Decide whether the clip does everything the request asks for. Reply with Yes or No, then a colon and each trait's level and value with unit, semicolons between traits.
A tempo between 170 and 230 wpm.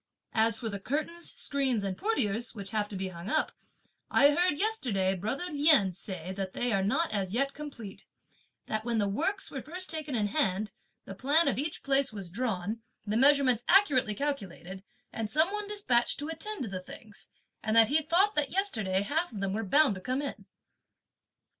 Yes: average, 190 wpm